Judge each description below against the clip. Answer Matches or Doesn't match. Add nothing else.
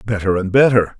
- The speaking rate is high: Doesn't match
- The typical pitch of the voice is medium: Doesn't match